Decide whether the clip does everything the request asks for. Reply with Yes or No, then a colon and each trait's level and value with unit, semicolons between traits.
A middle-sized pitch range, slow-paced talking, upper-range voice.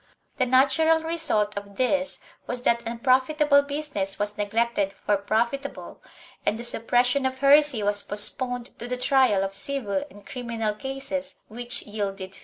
No: average, 4.9 semitones; average, 155 wpm; high, 245 Hz